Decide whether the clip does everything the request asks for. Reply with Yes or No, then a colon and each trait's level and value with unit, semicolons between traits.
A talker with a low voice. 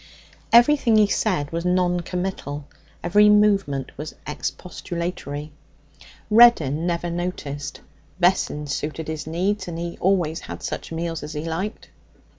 No: medium, 170 Hz